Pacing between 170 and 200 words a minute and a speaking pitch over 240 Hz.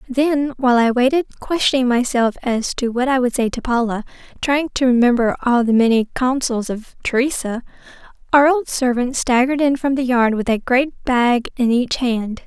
Yes: average, 185 wpm; very high, 250 Hz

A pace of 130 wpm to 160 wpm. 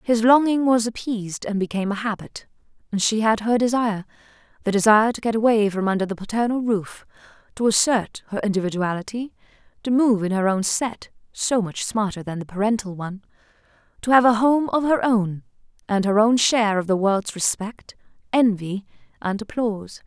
No: average, 170 wpm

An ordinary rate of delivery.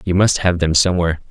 No: fast, 230 wpm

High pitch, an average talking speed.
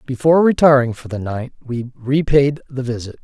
No: low, 130 Hz; average, 165 wpm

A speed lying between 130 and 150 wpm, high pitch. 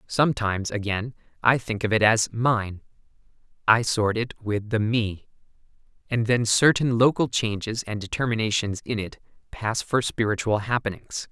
No: average, 145 wpm; low, 110 Hz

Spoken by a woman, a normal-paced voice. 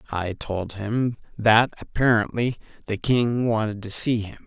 No: male; average, 150 wpm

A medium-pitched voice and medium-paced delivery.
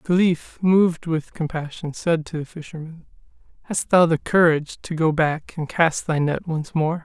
Yes: medium, 160 Hz; average, 190 wpm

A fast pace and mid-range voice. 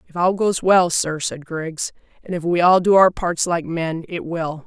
Yes: fast, 230 wpm; medium, 170 Hz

